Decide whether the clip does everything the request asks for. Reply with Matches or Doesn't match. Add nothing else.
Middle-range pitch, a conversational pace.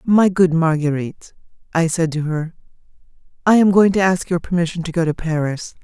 Matches